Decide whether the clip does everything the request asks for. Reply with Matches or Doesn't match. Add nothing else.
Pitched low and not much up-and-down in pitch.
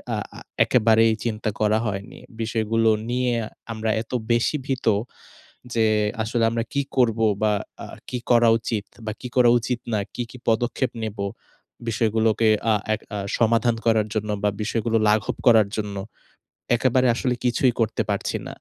Matches